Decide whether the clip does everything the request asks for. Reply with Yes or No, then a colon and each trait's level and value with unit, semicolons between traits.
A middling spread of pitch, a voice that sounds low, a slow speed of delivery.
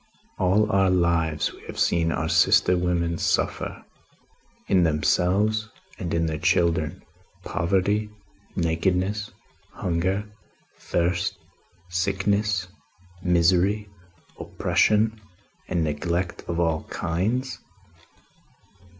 Yes: average, 3.0 semitones; very low, 90 Hz; slow, 90 wpm